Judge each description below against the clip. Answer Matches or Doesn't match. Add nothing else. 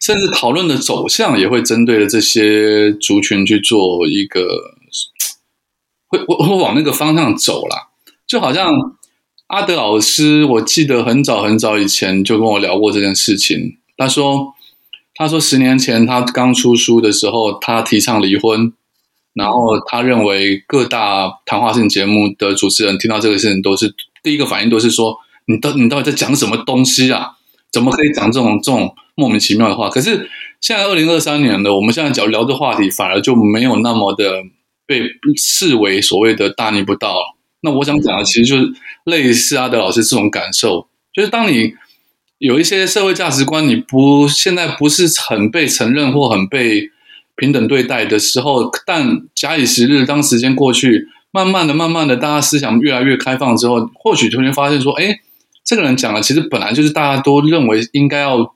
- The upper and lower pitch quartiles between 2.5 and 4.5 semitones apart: Doesn't match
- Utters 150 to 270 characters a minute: Doesn't match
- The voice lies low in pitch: Matches